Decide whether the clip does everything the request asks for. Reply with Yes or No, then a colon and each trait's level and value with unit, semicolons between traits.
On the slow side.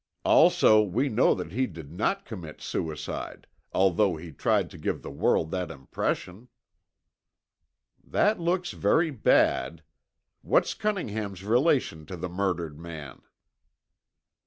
Yes: slow, 120 wpm